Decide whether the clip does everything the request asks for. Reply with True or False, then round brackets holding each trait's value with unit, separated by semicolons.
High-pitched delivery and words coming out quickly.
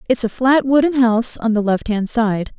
True (235 Hz; 230 wpm)